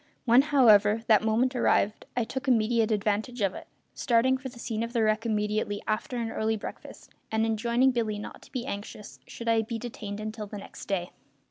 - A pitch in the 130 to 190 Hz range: No, high, 225 Hz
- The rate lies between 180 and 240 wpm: Yes, average, 200 wpm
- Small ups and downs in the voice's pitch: Yes, narrow, 2.1 semitones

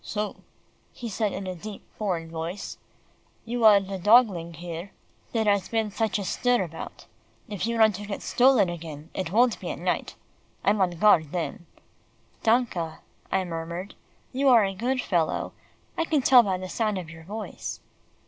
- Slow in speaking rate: No, average, 170 wpm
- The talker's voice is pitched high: Yes, high, 200 Hz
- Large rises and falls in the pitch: No, average, 4.5 semitones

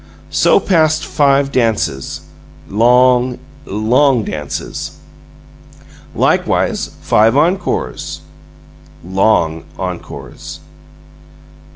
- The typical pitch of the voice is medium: No, low, 120 Hz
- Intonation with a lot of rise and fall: Yes, wide, 6.3 semitones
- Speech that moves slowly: Yes, slow, 60 wpm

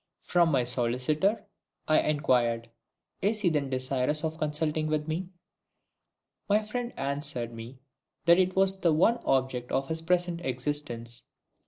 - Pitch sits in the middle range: Yes, medium, 150 Hz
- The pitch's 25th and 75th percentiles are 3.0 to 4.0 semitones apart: No, wide, 5.4 semitones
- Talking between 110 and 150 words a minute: Yes, average, 140 wpm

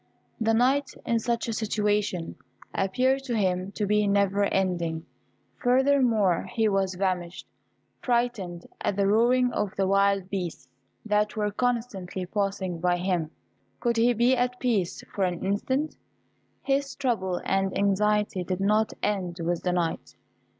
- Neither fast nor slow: Yes, average, 145 wpm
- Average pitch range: Yes, average, 4.1 semitones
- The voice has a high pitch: Yes, high, 205 Hz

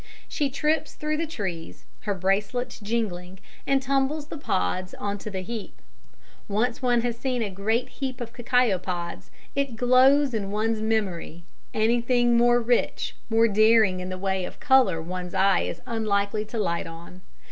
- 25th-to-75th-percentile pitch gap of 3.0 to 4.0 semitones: No, average, 4.5 semitones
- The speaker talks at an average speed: Yes, average, 165 wpm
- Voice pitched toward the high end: Yes, high, 220 Hz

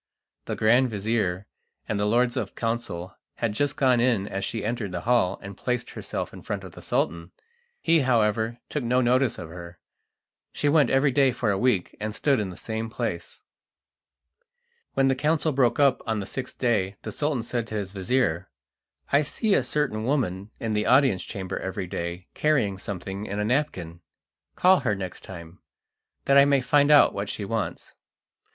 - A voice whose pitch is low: Yes, low, 115 Hz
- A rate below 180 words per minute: No, average, 185 wpm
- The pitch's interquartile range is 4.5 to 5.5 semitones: Yes, average, 5.1 semitones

